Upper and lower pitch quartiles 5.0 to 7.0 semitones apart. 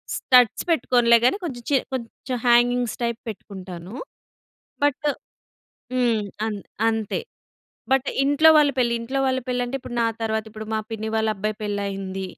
No: average, 2.9 semitones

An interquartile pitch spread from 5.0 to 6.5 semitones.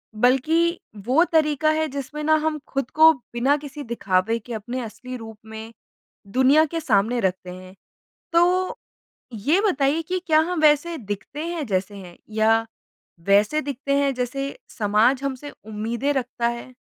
Yes: wide, 5.4 semitones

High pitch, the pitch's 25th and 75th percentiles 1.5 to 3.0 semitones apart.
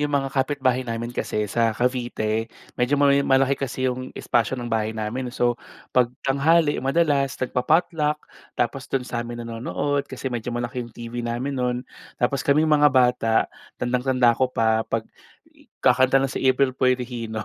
No: low, 125 Hz; narrow, 2.4 semitones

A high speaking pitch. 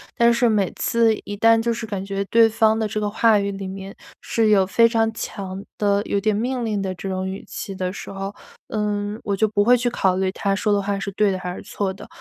Yes: high, 205 Hz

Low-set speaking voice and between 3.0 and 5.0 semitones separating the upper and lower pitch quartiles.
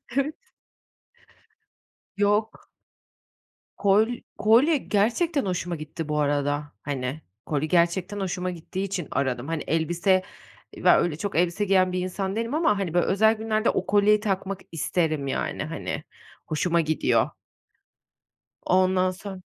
No: medium, 185 Hz; average, 4.1 semitones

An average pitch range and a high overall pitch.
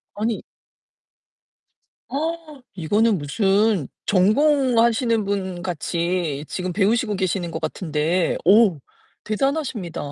Yes: average, 4.7 semitones; high, 200 Hz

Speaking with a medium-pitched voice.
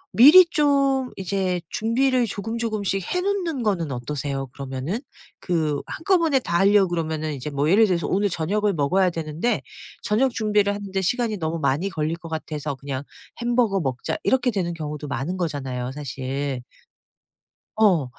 Yes: medium, 180 Hz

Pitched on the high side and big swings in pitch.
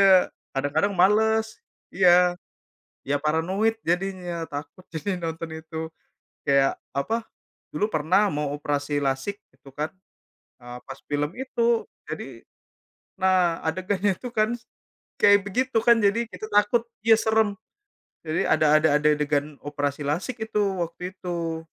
No: medium, 180 Hz; wide, 5.7 semitones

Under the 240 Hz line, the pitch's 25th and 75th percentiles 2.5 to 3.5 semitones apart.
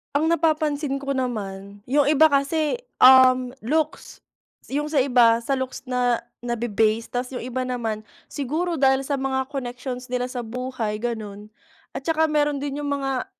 No: very high, 260 Hz; average, 2.9 semitones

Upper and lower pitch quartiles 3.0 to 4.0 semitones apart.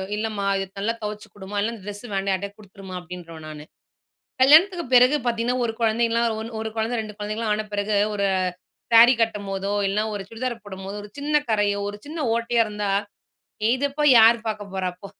No: narrow, 2.6 semitones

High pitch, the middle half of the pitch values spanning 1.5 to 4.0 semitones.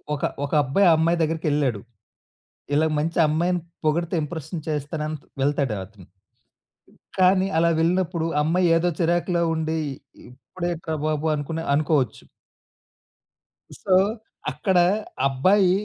No: medium, 160 Hz; average, 2.8 semitones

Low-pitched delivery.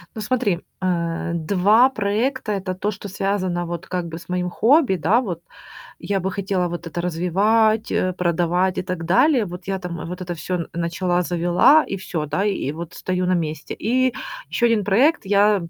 No: medium, 185 Hz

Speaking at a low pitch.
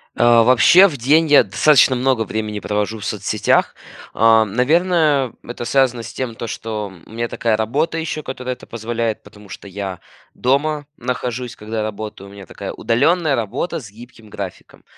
Yes: low, 115 Hz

